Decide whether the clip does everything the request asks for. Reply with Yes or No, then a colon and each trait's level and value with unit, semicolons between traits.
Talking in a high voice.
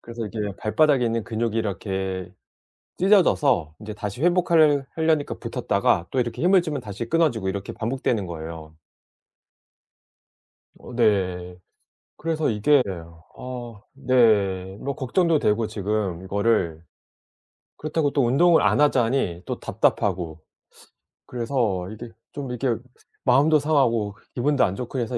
No: low, 115 Hz